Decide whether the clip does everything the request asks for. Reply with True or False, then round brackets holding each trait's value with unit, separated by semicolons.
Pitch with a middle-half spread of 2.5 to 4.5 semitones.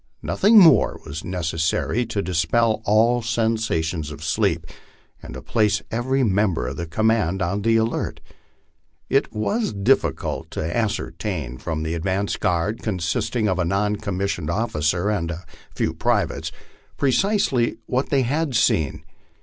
False (5.5 semitones)